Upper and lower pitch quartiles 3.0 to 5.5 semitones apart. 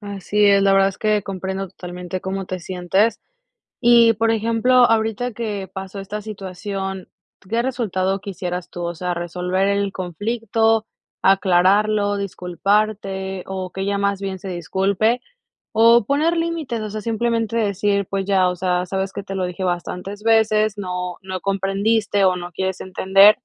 No: narrow, 2.4 semitones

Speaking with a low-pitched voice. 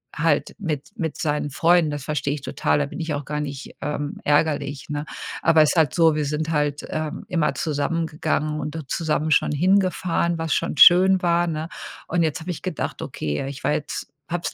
No: medium, 155 Hz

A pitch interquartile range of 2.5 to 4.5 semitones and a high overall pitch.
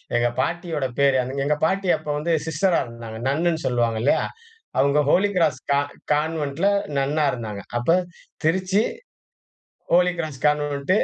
No: average, 3.9 semitones; medium, 150 Hz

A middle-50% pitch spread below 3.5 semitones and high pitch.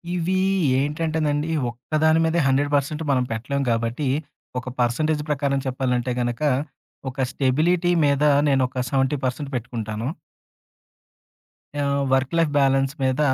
No: average, 2.9 semitones; medium, 140 Hz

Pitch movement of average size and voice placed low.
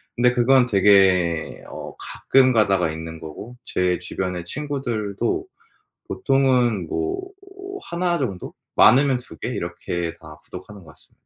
No: wide, 6.2 semitones; low, 100 Hz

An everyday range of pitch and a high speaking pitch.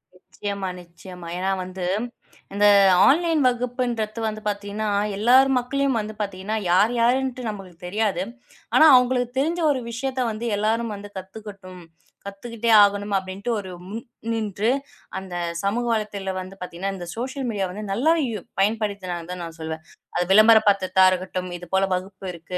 Yes: average, 3.8 semitones; high, 205 Hz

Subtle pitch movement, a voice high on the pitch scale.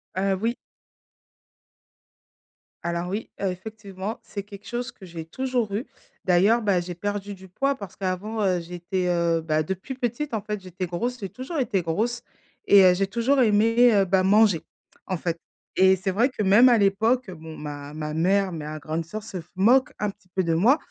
No: average, 4.0 semitones; high, 195 Hz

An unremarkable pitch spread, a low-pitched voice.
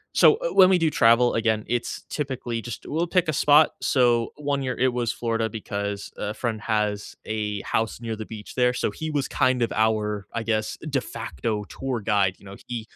Yes: average, 3.3 semitones; low, 115 Hz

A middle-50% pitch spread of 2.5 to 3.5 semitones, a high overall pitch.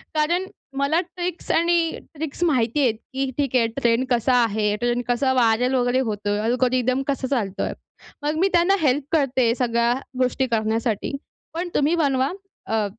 No: average, 4.1 semitones; very high, 255 Hz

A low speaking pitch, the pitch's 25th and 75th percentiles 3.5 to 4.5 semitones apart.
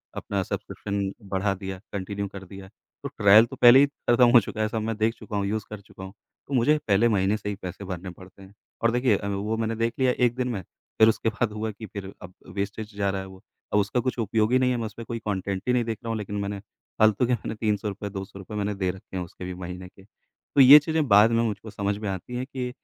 No: low, 105 Hz; average, 2.9 semitones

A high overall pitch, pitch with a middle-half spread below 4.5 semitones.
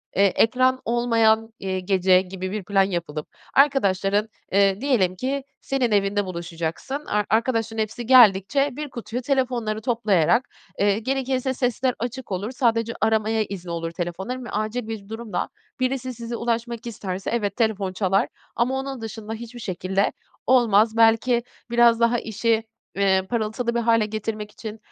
Yes: high, 225 Hz; average, 3.5 semitones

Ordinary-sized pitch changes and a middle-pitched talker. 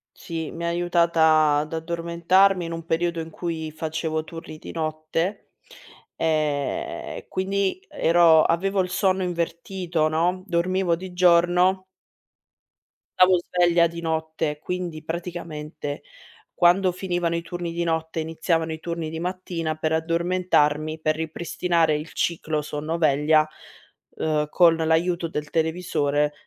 No: narrow, 1.9 semitones; medium, 165 Hz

